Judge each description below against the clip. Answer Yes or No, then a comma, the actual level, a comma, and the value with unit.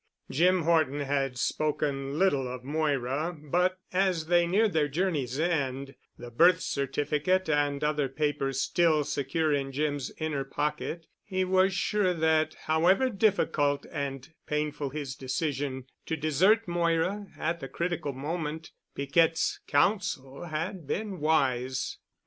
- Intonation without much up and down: No, average, 3.8 semitones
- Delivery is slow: Yes, slow, 130 wpm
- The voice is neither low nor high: Yes, medium, 155 Hz